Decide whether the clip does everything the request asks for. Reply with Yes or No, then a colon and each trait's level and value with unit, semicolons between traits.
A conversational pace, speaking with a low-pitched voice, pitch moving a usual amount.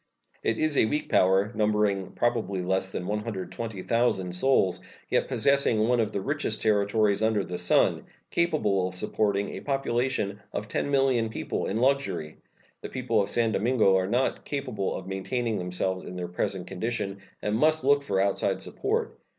Yes: average, 165 wpm; low, 105 Hz; average, 4.2 semitones